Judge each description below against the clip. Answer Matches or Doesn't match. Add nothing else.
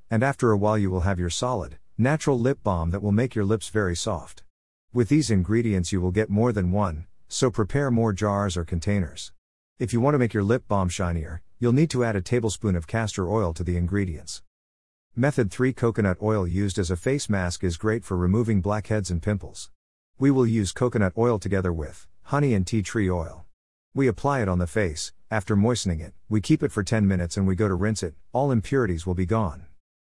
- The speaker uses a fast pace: Matches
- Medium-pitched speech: Doesn't match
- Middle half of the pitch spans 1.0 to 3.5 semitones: Doesn't match